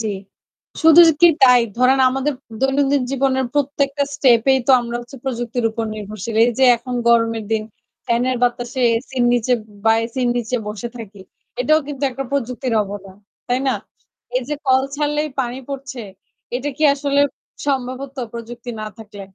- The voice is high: Yes, very high, 255 Hz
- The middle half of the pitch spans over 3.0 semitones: No, average, 2.7 semitones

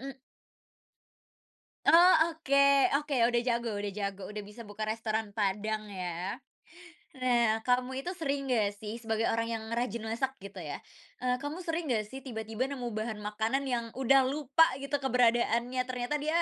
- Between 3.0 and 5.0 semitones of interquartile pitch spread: Yes, average, 3.7 semitones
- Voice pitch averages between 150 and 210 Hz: No, high, 235 Hz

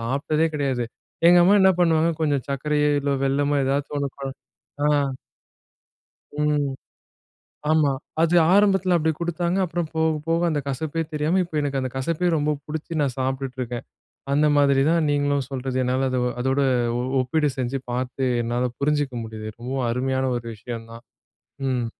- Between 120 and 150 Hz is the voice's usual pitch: Yes, medium, 140 Hz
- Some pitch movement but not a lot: Yes, average, 3.4 semitones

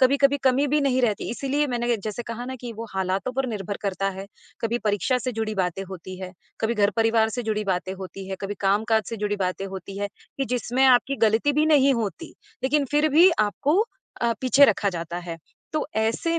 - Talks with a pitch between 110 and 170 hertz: No, high, 225 Hz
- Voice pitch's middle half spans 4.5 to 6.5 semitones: Yes, average, 5.0 semitones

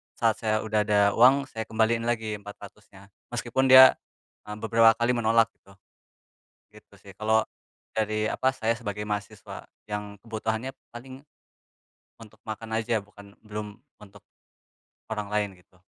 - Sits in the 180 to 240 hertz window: No, low, 110 Hz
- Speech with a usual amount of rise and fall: No, narrow, 1.8 semitones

